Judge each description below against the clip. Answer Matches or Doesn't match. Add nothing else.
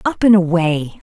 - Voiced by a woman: Matches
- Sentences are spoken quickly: Doesn't match